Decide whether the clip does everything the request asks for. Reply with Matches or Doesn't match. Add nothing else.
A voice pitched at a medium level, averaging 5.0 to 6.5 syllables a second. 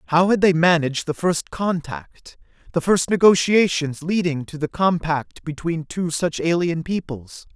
Doesn't match